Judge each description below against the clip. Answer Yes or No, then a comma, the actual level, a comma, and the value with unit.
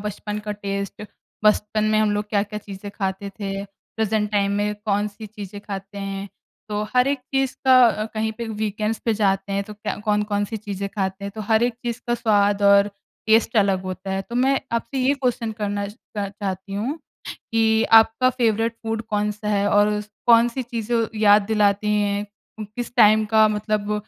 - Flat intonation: Yes, narrow, 1.7 semitones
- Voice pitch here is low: No, high, 210 Hz